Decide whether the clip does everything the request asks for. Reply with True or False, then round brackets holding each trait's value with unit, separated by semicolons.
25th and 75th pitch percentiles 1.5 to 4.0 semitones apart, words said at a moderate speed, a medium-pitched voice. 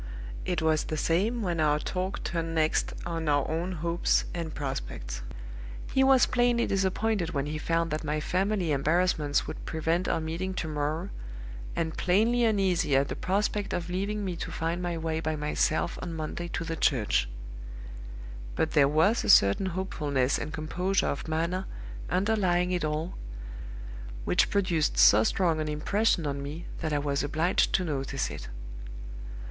True (3.4 semitones; 165 wpm; 165 Hz)